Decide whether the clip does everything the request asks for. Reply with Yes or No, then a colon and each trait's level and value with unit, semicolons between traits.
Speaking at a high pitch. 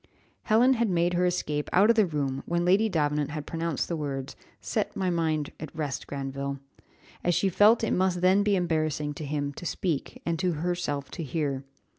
No: medium, 165 Hz